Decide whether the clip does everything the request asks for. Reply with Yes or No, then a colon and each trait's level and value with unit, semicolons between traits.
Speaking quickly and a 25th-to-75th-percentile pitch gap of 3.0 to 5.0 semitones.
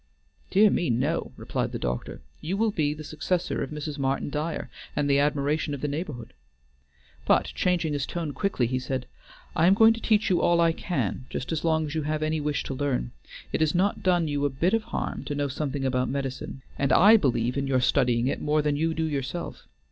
Yes: fast, 220 wpm; average, 3.6 semitones